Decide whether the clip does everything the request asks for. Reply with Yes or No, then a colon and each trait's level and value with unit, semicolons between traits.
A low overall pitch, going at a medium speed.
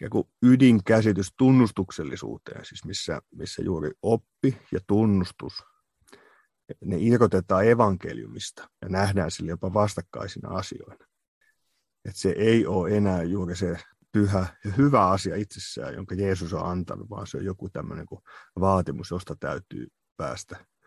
Yes: low, 100 Hz; average, 125 wpm